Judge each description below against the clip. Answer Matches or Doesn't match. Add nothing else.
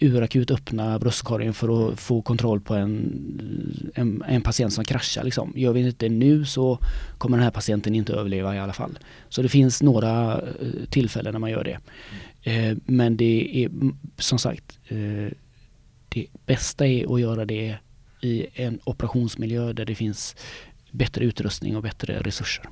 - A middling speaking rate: Matches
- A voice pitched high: Doesn't match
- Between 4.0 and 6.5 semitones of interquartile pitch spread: Doesn't match